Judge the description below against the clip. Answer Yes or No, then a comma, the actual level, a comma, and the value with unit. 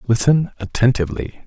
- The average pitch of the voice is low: Yes, low, 115 Hz